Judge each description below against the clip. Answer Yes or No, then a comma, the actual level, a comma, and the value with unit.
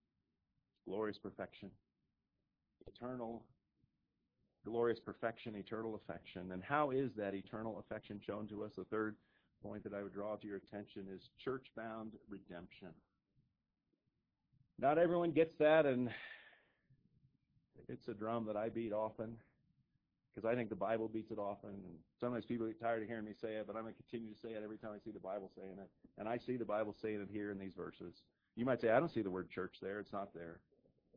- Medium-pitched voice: No, low, 110 Hz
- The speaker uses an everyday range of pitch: No, narrow, 2.2 semitones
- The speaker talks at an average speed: Yes, average, 190 wpm